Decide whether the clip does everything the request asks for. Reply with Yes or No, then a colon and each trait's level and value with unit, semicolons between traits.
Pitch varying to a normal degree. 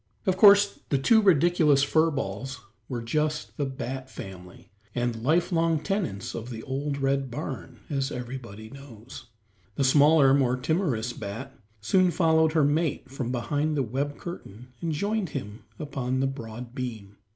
Yes: average, 4.3 semitones